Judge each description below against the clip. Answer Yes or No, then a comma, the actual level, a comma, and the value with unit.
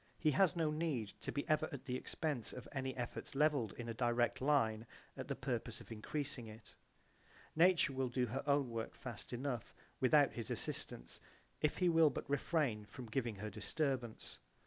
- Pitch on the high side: No, low, 130 Hz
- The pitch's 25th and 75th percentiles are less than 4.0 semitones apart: No, average, 4.3 semitones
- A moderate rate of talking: Yes, average, 180 wpm